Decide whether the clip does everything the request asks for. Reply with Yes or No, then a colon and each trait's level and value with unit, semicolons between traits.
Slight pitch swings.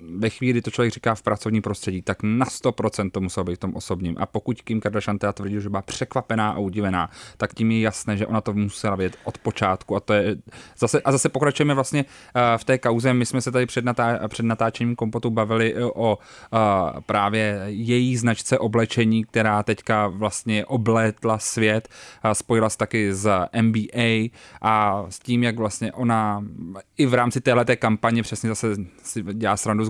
Yes: narrow, 2.2 semitones